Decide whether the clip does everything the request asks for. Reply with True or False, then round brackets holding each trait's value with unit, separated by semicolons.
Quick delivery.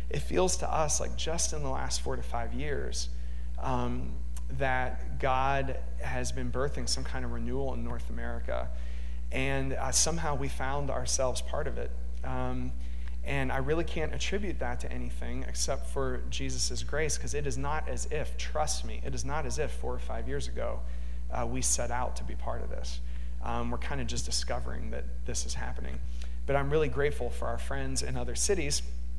False (195 wpm)